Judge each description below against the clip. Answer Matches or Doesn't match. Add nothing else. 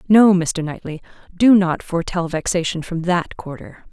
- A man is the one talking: Doesn't match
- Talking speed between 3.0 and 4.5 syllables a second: Doesn't match